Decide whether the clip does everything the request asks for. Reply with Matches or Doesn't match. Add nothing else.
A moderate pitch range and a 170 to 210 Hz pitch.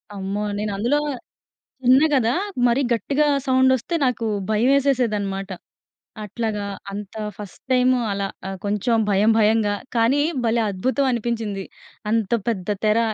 Doesn't match